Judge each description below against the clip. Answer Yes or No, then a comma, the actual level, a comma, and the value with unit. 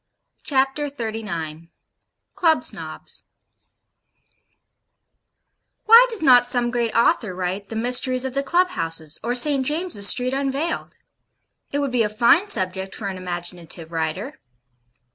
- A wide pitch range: Yes, wide, 6.8 semitones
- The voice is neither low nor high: No, high, 240 Hz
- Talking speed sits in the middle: No, slow, 125 wpm